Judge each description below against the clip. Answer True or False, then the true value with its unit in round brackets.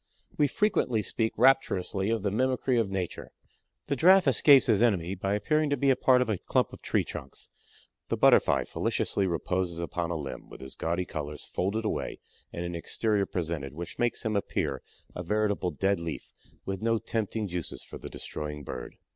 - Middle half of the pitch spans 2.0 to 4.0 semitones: False (5.2 semitones)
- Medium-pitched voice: False (100 Hz)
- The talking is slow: False (185 wpm)